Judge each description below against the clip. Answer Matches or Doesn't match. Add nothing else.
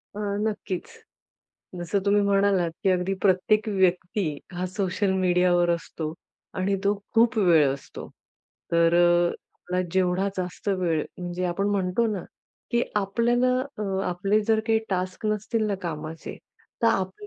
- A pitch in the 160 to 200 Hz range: Matches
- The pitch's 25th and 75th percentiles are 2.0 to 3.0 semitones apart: Matches